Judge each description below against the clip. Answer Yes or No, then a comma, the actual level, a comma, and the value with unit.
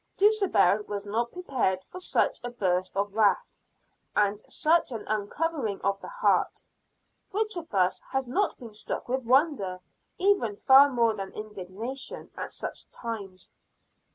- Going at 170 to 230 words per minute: No, average, 145 wpm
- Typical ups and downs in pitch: No, wide, 7.2 semitones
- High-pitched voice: Yes, high, 230 Hz